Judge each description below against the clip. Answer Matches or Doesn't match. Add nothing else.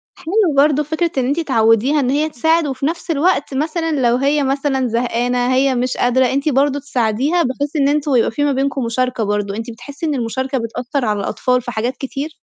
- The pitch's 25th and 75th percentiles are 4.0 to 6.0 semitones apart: Doesn't match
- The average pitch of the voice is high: Matches